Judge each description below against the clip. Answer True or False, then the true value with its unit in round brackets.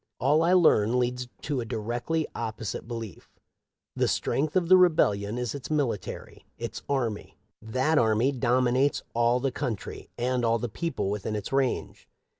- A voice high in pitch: False (125 Hz)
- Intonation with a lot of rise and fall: False (3.9 semitones)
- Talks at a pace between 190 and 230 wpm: False (160 wpm)